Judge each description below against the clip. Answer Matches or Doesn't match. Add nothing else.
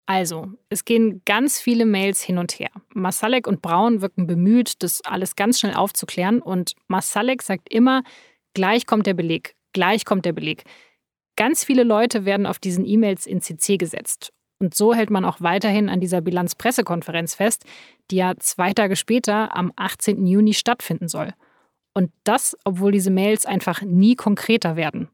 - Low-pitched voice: Doesn't match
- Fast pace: Doesn't match